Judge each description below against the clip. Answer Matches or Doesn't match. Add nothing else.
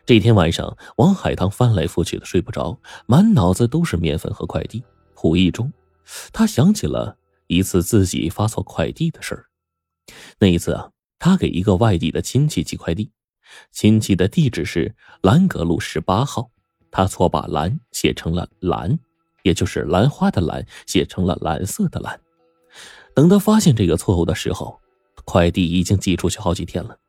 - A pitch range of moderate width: Doesn't match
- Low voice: Matches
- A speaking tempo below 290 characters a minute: Matches